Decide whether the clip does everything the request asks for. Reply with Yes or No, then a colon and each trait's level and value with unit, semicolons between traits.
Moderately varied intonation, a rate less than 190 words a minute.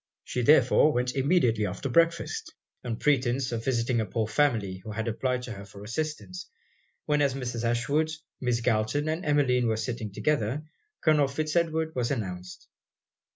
Yes: average, 4.7 semitones; average, 160 wpm